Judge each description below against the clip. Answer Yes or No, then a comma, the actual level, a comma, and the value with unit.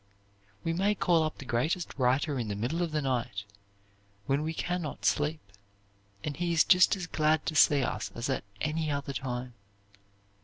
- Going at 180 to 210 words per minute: Yes, average, 185 wpm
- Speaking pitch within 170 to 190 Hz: No, medium, 150 Hz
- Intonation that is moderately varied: Yes, average, 4.2 semitones